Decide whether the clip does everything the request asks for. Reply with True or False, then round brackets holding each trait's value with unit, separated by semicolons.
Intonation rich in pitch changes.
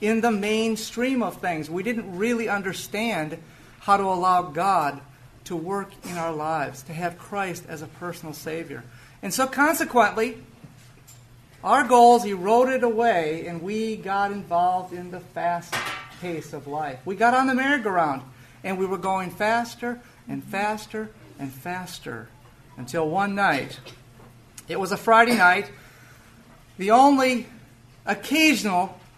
True (7.4 semitones)